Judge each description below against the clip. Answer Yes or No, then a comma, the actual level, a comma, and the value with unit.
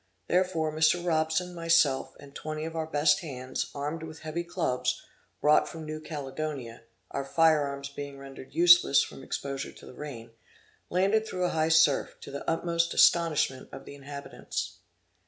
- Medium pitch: Yes, medium, 155 Hz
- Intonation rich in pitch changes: No, average, 3.1 semitones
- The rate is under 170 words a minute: Yes, average, 160 wpm